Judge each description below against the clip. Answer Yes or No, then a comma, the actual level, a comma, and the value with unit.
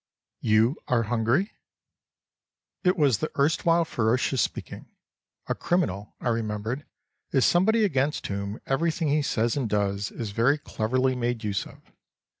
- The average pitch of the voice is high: No, low, 125 Hz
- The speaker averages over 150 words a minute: No, slow, 135 wpm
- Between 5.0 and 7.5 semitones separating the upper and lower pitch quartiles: Yes, wide, 5.5 semitones